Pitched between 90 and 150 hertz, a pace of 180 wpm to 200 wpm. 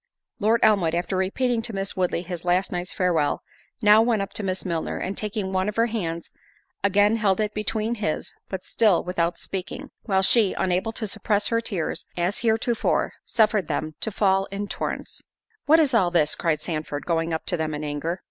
No: high, 195 Hz; average, 190 wpm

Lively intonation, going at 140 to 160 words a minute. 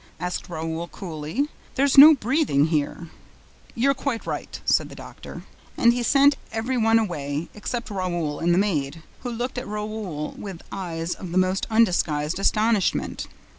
Yes: wide, 6.2 semitones; average, 155 wpm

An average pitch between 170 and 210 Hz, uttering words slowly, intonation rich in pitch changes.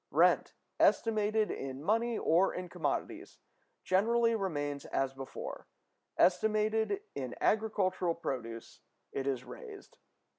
Yes: high, 190 Hz; slow, 105 wpm; wide, 7.6 semitones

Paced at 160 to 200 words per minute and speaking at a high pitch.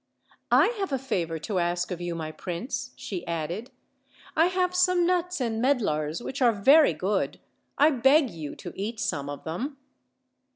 Yes: average, 170 wpm; high, 220 Hz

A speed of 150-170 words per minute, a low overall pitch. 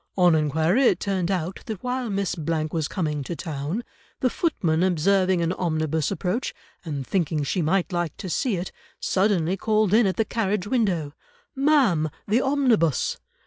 No: average, 165 wpm; medium, 185 Hz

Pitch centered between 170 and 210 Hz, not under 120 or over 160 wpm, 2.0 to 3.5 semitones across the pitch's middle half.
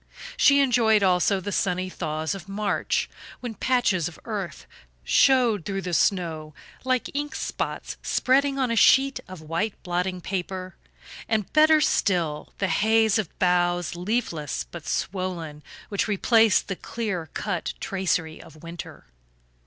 No: high, 190 Hz; slow, 135 wpm; average, 4.3 semitones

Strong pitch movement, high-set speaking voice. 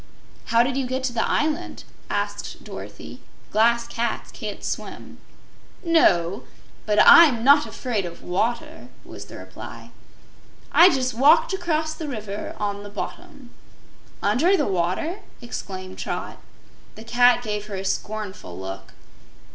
Yes: wide, 6.1 semitones; high, 235 Hz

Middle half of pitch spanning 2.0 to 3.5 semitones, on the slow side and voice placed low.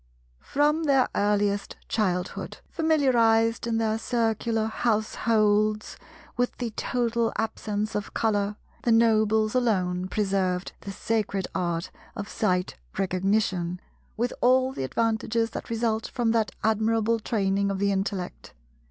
No: narrow, 2.4 semitones; slow, 120 wpm; high, 220 Hz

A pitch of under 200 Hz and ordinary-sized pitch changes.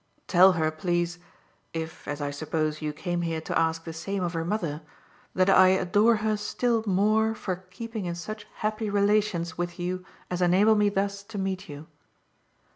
Yes: medium, 185 Hz; average, 3.8 semitones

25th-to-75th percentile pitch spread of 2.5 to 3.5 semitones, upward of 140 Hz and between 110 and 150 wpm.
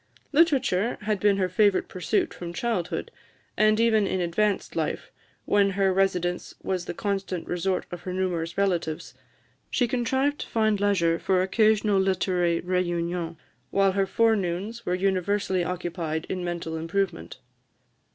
Yes: average, 2.9 semitones; high, 190 Hz; average, 140 wpm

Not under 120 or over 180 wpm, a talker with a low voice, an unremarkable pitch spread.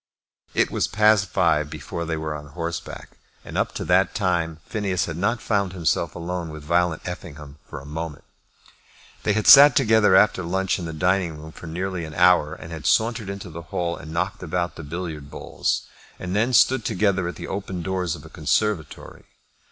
No: average, 190 wpm; very low, 90 Hz; average, 3.3 semitones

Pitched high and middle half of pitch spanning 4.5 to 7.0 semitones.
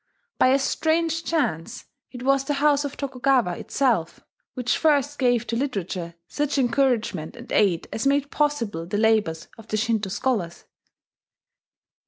Yes: very high, 250 Hz; average, 4.8 semitones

